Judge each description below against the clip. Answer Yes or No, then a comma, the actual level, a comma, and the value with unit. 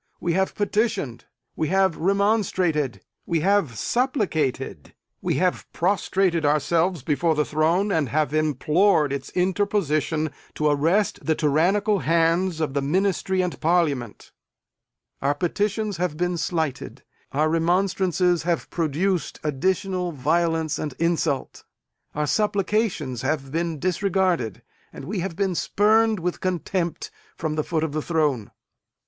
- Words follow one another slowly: Yes, slow, 130 wpm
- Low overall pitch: No, medium, 170 Hz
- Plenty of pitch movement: No, average, 3.9 semitones